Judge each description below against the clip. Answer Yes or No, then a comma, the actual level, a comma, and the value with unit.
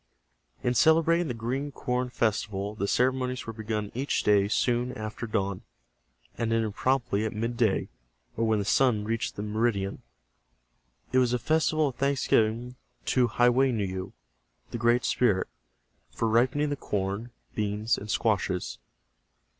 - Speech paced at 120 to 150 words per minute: Yes, average, 145 wpm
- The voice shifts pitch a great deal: No, average, 3.1 semitones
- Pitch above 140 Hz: No, low, 115 Hz